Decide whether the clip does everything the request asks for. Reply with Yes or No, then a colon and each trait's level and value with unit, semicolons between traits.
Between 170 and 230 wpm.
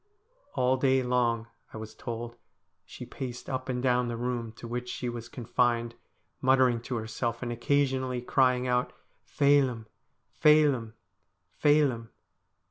No: slow, 135 wpm